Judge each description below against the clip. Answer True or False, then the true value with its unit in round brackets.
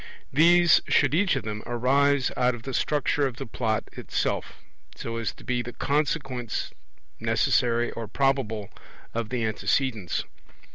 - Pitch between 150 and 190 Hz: False (125 Hz)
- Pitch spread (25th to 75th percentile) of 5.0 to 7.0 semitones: False (3.6 semitones)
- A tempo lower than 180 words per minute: True (145 wpm)